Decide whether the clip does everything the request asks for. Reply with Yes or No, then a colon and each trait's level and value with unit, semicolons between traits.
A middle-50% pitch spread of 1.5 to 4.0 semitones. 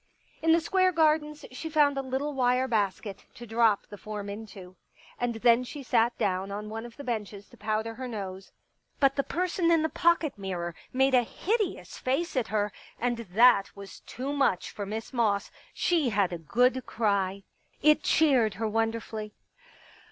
No: average, 5.1 semitones